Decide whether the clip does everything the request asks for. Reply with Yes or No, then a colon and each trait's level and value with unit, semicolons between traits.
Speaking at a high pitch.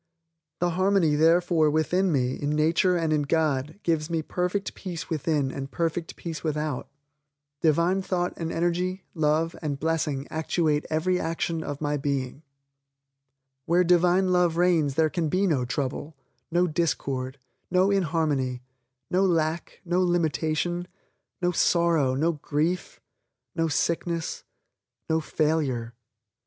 No: medium, 160 Hz